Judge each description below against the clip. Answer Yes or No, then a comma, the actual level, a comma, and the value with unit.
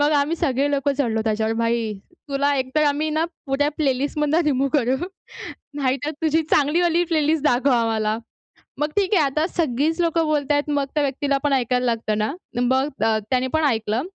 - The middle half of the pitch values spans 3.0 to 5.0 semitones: Yes, average, 3.4 semitones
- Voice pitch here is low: No, very high, 280 Hz